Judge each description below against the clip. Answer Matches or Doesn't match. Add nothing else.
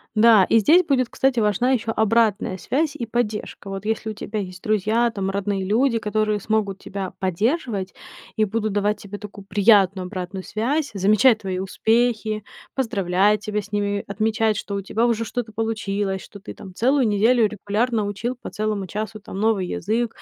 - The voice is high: Matches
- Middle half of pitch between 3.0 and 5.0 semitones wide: Doesn't match